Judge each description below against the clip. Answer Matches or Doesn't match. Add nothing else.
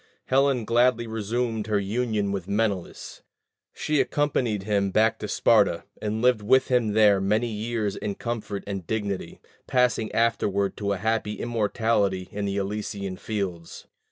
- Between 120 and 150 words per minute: Matches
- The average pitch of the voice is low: Matches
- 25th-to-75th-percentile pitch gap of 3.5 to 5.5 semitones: Doesn't match